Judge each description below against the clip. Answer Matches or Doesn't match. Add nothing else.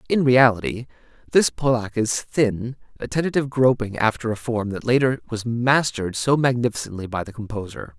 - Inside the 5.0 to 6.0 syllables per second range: Matches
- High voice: Doesn't match